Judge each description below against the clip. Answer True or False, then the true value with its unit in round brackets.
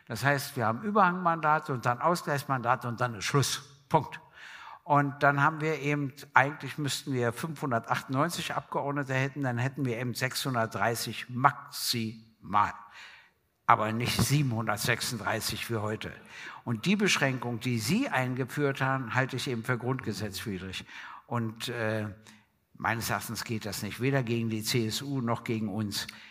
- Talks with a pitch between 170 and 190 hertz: False (125 Hz)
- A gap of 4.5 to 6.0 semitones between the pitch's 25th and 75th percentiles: False (3.9 semitones)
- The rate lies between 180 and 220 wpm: False (140 wpm)